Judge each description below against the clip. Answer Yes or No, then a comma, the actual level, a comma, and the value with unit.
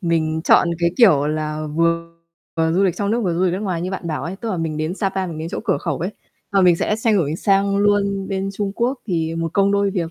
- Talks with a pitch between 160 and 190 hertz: Yes, medium, 185 Hz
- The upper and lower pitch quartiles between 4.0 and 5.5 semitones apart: No, average, 3.3 semitones